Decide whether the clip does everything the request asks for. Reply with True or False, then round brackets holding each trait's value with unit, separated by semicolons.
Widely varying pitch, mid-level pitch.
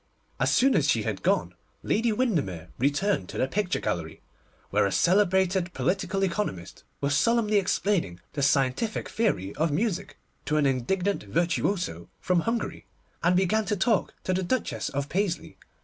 True (6.6 semitones; 180 Hz)